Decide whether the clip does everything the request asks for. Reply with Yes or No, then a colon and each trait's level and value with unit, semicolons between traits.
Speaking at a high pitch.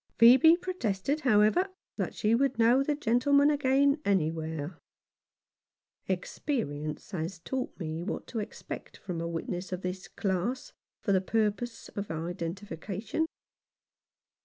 Yes: high, 210 Hz